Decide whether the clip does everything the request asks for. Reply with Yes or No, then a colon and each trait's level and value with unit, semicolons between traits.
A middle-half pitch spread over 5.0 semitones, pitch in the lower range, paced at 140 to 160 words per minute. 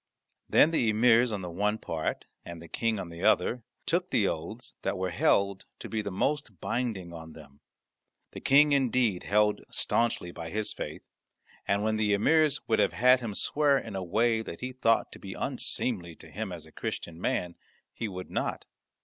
No: wide, 5.4 semitones; low, 105 Hz; average, 190 wpm